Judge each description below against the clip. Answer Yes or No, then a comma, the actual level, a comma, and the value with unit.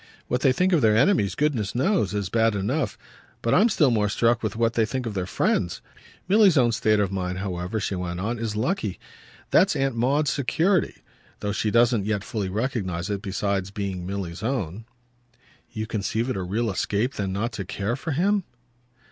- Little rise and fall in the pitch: No, average, 4.6 semitones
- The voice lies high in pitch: No, low, 110 Hz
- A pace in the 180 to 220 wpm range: Yes, average, 190 wpm